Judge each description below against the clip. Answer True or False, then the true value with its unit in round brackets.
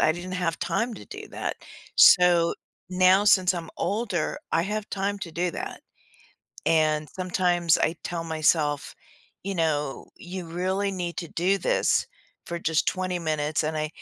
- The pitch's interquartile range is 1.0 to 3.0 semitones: True (2.5 semitones)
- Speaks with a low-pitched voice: False (175 Hz)